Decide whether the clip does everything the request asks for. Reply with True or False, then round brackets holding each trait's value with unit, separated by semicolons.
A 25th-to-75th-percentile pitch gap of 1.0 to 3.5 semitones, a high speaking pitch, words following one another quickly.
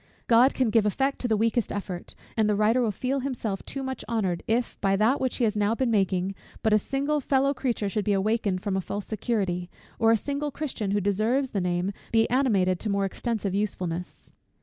False (4.2 semitones; 215 Hz; 215 wpm)